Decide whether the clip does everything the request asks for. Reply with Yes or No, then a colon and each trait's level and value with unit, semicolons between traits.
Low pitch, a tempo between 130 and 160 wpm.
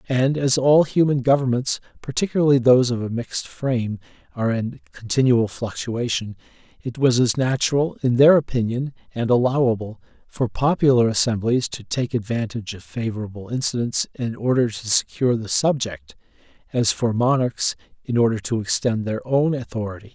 Yes: low, 120 Hz; average, 145 wpm